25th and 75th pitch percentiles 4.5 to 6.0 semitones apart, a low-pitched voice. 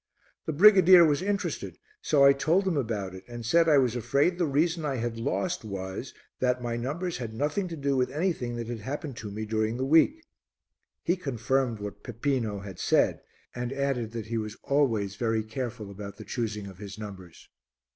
Yes: average, 5.3 semitones; low, 125 Hz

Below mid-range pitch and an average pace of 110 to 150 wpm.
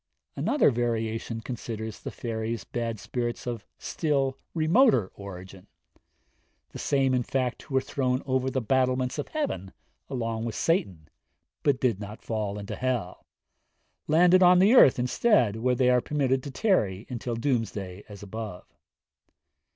Yes: low, 125 Hz; average, 145 wpm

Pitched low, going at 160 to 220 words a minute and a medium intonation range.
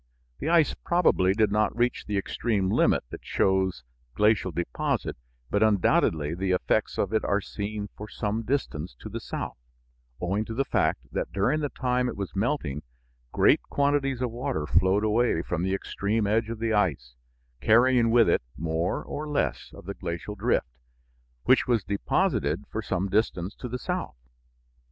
Yes: low, 105 Hz; average, 170 wpm; average, 4.5 semitones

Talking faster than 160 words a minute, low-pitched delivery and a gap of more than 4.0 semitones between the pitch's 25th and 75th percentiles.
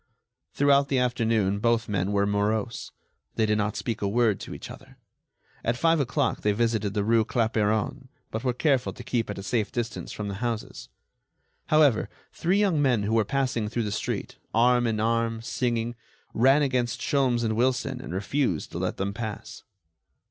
No: average, 180 wpm; low, 115 Hz; average, 3.0 semitones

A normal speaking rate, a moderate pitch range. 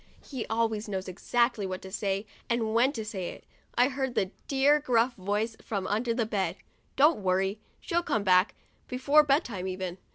Yes: average, 175 wpm; average, 4.7 semitones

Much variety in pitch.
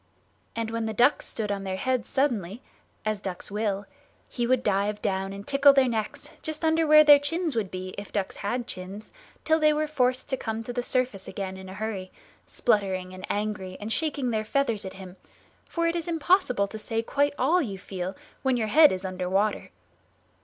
Yes: wide, 6.0 semitones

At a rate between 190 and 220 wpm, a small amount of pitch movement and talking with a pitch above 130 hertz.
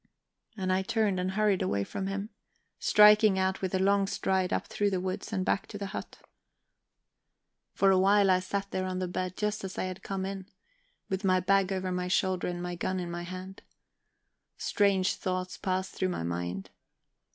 Yes: average, 195 wpm; narrow, 1.3 semitones; high, 190 Hz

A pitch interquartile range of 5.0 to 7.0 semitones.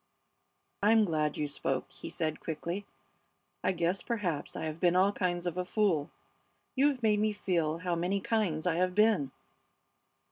No: average, 4.3 semitones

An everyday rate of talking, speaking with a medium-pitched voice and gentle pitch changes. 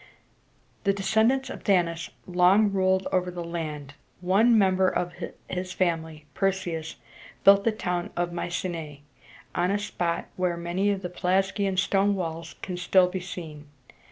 Yes: average, 155 wpm; medium, 180 Hz; narrow, 2.3 semitones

